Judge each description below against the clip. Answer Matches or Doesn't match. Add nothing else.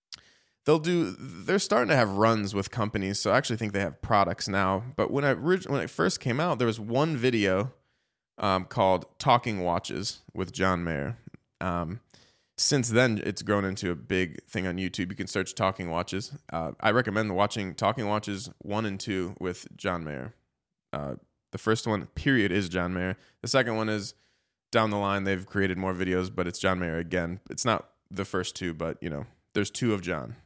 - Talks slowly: Doesn't match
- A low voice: Matches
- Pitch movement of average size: Matches